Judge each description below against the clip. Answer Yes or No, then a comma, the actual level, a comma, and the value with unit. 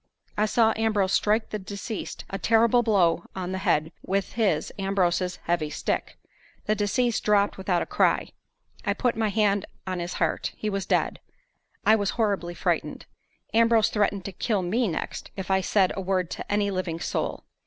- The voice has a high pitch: Yes, high, 200 Hz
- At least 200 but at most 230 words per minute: No, average, 175 wpm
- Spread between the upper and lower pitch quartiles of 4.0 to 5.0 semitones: No, average, 2.7 semitones